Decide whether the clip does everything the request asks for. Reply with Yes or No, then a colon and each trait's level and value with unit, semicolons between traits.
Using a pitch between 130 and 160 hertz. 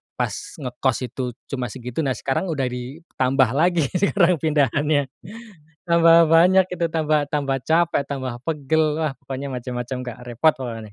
Yes: medium, 140 Hz